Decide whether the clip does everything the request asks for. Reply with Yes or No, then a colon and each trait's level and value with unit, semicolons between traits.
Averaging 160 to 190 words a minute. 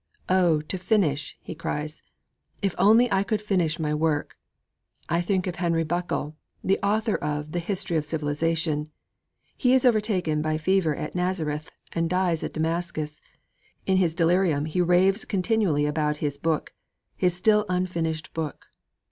No: average, 150 wpm